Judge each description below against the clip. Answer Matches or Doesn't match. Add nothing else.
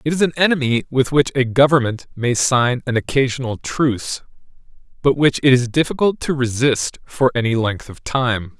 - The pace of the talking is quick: Doesn't match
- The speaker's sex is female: Doesn't match